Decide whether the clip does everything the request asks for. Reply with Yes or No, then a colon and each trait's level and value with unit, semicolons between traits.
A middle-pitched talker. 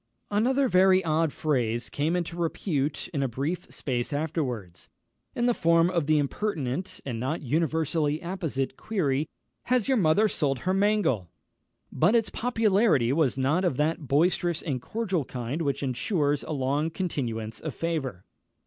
Yes: medium, 155 Hz